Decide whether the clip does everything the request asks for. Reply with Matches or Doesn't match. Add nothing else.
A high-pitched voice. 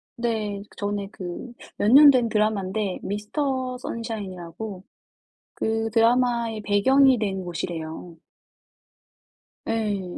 Matches